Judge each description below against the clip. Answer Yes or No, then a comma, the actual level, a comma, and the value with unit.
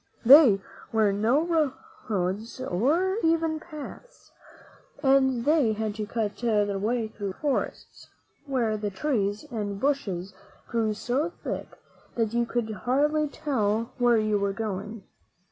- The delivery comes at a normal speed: No, slow, 130 wpm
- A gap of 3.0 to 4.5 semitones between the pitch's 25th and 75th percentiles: No, average, 5.1 semitones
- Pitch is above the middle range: Yes, high, 230 Hz